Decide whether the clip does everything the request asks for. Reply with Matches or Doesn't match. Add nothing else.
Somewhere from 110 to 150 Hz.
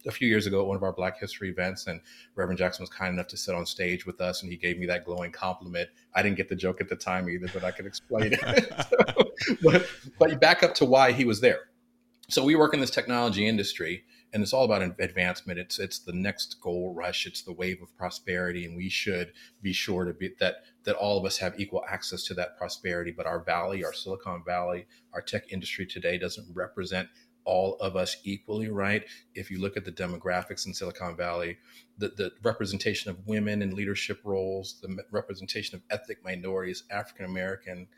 Doesn't match